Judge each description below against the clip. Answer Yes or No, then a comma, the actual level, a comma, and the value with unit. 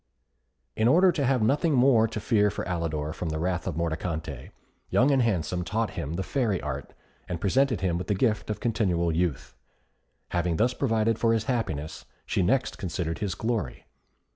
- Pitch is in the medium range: No, low, 100 Hz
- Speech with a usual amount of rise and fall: No, wide, 5.8 semitones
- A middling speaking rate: Yes, average, 180 wpm